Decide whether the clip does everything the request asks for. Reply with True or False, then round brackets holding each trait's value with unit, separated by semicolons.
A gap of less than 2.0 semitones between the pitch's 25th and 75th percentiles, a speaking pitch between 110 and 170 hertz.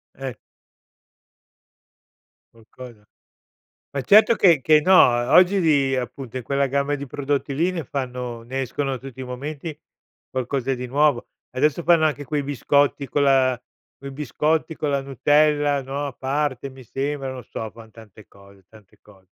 False (2.7 semitones; 135 Hz)